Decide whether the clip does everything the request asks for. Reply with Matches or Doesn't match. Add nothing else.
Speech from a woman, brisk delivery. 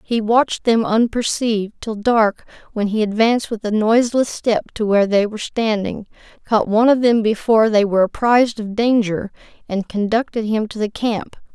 Doesn't match